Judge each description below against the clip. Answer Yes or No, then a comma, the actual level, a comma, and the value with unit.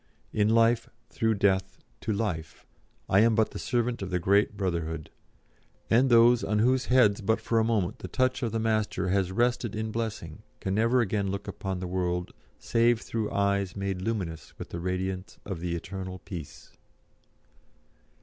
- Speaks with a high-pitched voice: No, low, 100 Hz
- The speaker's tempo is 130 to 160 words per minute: No, average, 170 wpm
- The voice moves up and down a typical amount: Yes, average, 3.6 semitones